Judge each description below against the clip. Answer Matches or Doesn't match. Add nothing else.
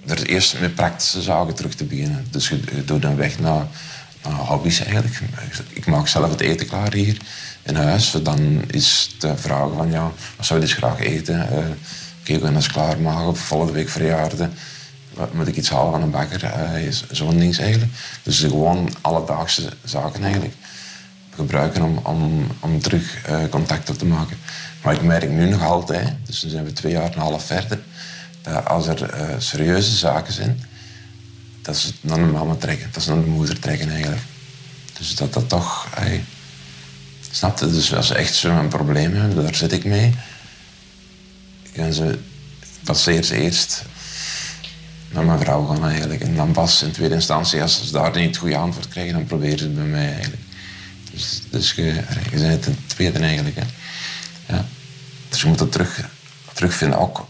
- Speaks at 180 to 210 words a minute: Matches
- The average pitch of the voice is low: Matches